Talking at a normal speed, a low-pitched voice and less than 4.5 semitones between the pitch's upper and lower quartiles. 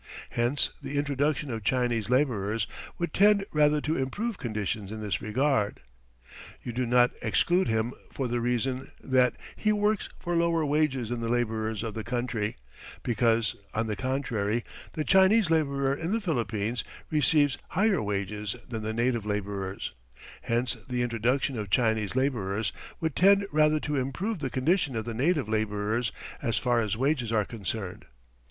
No: average, 160 wpm; low, 125 Hz; average, 5.1 semitones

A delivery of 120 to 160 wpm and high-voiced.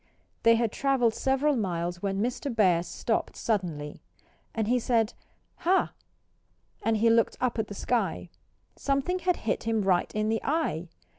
Yes: average, 155 wpm; high, 225 Hz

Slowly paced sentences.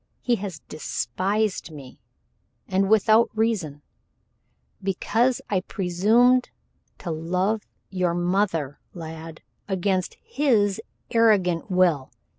Yes: slow, 90 wpm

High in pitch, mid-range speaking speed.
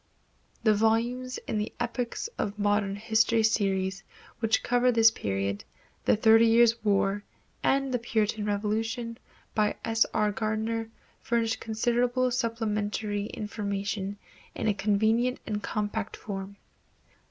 No: high, 220 Hz; slow, 120 wpm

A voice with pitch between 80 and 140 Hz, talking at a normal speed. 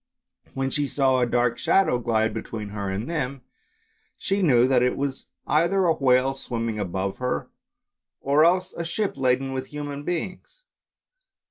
Yes: low, 135 Hz; average, 155 wpm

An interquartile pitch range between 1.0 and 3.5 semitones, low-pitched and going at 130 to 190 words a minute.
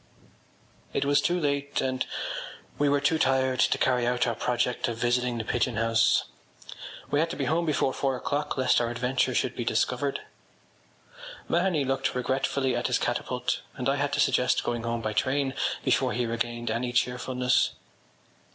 Yes: narrow, 2.5 semitones; low, 130 Hz; average, 170 wpm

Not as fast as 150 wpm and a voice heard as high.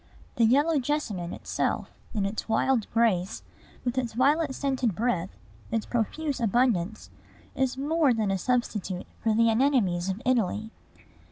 Yes: average, 140 wpm; high, 235 Hz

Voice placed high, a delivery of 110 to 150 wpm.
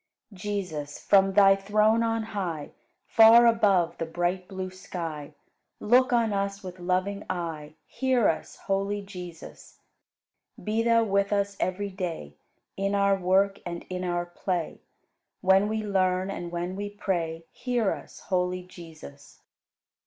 Yes: high, 195 Hz; average, 140 wpm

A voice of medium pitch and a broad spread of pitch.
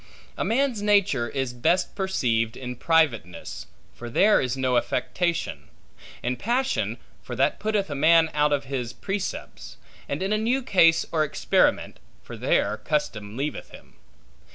Yes: medium, 150 Hz; wide, 7.7 semitones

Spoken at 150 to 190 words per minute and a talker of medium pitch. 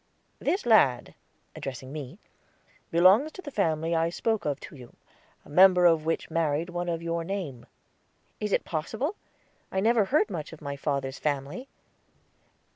Yes: average, 155 wpm; medium, 165 Hz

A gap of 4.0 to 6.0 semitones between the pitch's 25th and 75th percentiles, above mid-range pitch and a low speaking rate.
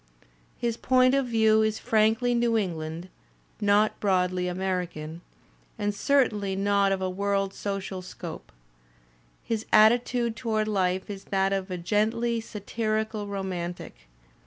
No: average, 3.0 semitones; high, 205 Hz; slow, 120 wpm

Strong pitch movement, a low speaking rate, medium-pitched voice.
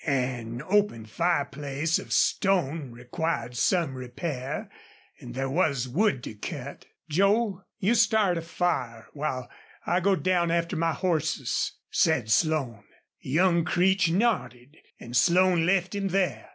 Yes: wide, 6.2 semitones; slow, 130 wpm; medium, 160 Hz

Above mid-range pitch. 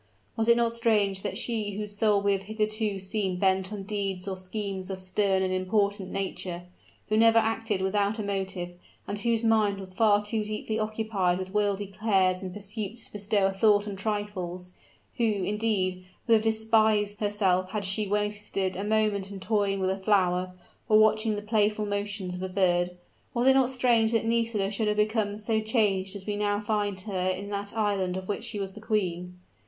Yes: high, 205 Hz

